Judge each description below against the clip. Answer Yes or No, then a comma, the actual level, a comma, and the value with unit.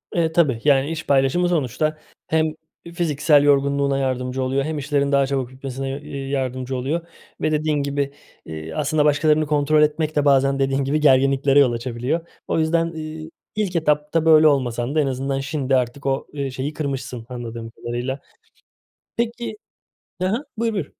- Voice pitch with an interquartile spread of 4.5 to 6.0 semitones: No, narrow, 2.6 semitones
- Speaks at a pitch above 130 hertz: Yes, medium, 140 Hz